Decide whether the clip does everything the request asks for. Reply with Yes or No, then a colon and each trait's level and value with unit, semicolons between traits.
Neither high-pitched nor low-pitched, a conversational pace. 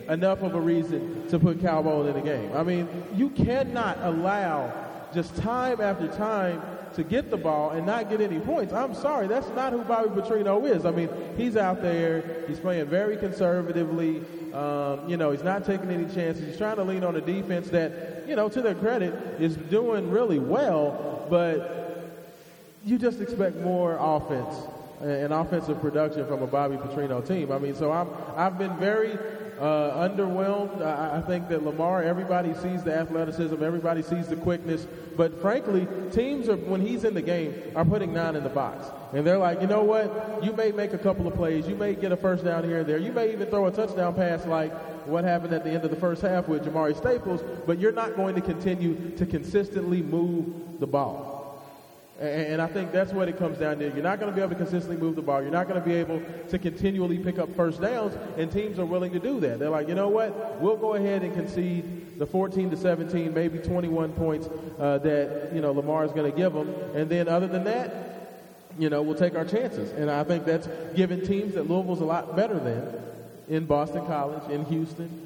No: medium, 170 Hz; fast, 215 wpm